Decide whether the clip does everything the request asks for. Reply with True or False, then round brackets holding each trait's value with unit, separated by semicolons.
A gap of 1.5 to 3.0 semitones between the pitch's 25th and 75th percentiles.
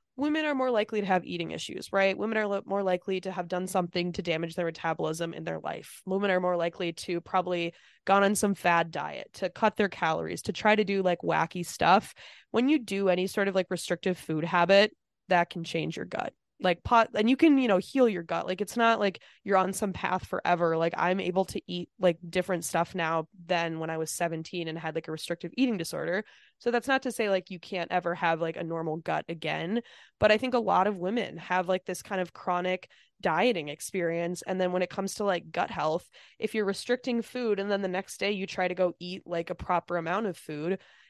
True (2.7 semitones)